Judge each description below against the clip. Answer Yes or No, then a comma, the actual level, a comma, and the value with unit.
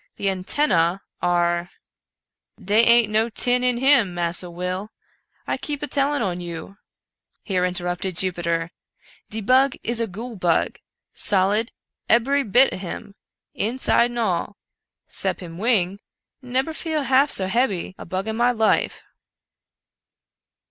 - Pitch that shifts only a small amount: No, wide, 5.4 semitones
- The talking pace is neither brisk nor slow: Yes, average, 150 wpm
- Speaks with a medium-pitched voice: No, high, 210 Hz